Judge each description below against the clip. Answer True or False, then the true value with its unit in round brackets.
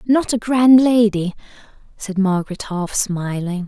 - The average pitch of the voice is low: False (205 Hz)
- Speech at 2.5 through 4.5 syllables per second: True (4.1 syllables/s)